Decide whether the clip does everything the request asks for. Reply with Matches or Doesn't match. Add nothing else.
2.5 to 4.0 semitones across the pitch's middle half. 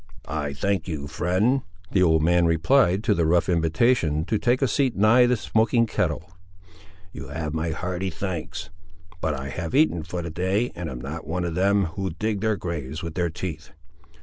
Doesn't match